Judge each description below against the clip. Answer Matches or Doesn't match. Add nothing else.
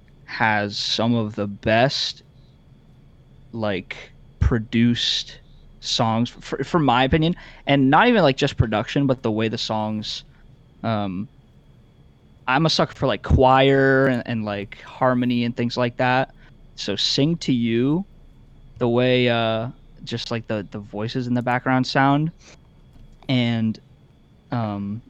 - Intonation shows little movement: Doesn't match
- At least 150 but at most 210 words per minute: Doesn't match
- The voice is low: Matches